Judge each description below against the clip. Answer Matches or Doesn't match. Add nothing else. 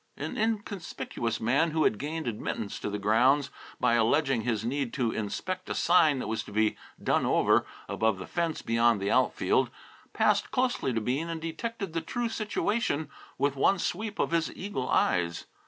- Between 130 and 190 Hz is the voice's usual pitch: Matches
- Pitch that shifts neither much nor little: Doesn't match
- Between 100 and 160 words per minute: Doesn't match